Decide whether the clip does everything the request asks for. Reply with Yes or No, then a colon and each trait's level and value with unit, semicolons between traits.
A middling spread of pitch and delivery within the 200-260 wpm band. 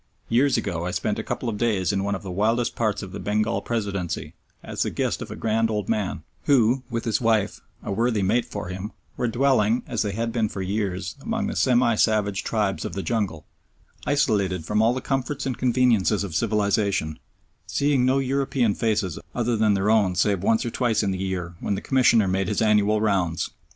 Yes: average, 3.3 semitones; fast, 205 wpm